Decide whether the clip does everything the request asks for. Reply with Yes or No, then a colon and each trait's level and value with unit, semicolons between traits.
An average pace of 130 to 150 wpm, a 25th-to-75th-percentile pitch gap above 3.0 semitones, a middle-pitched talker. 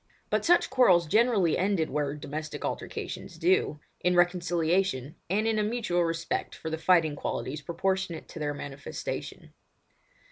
Yes: average, 140 wpm; average, 4.0 semitones; medium, 170 Hz